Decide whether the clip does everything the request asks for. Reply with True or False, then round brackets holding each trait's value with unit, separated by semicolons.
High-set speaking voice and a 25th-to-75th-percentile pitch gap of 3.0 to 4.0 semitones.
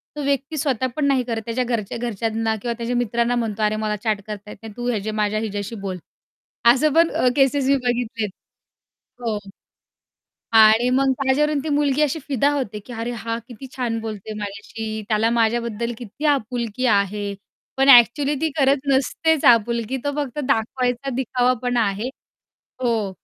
True (240 Hz; 3.6 semitones)